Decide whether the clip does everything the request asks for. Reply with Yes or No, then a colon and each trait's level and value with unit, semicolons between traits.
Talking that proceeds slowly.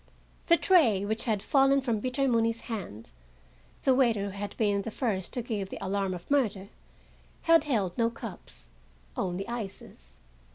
No: average, 150 wpm